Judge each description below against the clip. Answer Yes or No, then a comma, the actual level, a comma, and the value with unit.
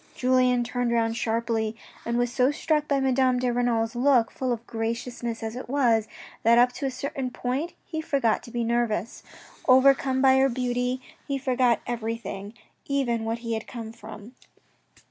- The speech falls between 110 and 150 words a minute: No, average, 175 wpm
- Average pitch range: No, narrow, 2.2 semitones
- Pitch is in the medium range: No, high, 245 Hz